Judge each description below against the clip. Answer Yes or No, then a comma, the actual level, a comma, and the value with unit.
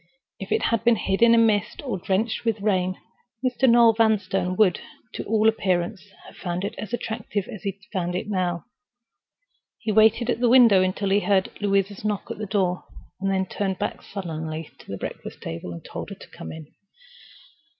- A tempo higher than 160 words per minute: Yes, average, 185 wpm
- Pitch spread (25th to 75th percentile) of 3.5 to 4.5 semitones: No, average, 3.1 semitones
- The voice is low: No, high, 200 Hz